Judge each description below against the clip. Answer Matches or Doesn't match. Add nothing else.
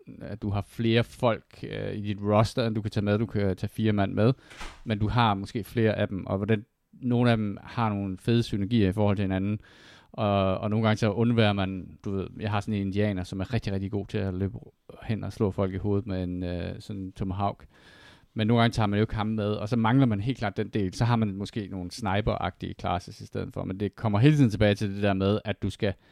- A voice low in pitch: Matches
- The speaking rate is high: Matches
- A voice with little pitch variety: Matches